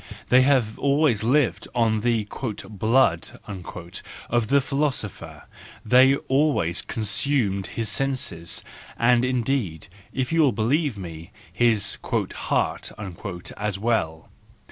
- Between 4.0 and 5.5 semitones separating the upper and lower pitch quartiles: Yes, average, 4.9 semitones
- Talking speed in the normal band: No, slow, 120 wpm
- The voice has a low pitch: Yes, low, 115 Hz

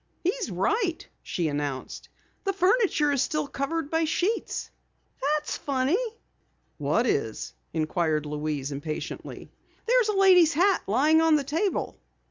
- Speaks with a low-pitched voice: No, very high, 295 Hz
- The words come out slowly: Yes, slow, 130 wpm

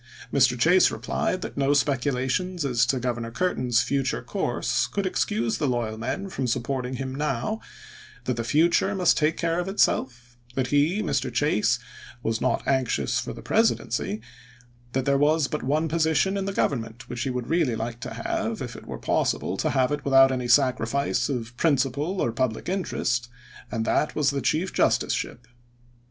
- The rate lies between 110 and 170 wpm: No, average, 180 wpm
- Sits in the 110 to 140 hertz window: Yes, low, 135 Hz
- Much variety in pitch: No, average, 4.2 semitones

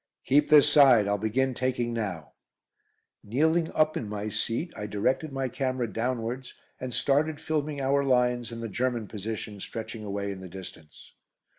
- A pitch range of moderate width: Yes, average, 4.5 semitones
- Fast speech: No, average, 160 wpm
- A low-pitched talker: Yes, low, 120 Hz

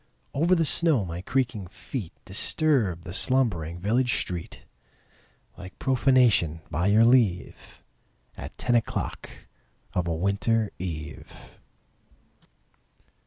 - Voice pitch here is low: Yes, low, 100 Hz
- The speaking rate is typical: No, slow, 105 wpm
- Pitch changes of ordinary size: No, wide, 6.5 semitones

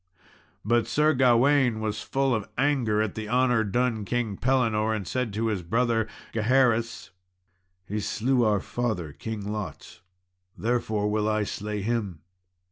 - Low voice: Yes, low, 115 Hz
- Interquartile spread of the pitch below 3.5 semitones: Yes, narrow, 2.6 semitones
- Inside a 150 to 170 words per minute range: No, average, 140 wpm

